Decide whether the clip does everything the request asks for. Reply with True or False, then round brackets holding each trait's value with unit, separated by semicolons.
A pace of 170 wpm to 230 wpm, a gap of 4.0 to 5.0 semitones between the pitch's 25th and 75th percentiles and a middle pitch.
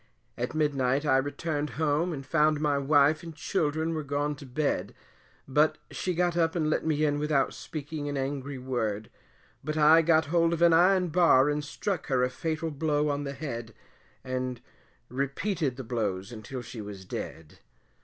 False (175 wpm; 3.1 semitones; 145 Hz)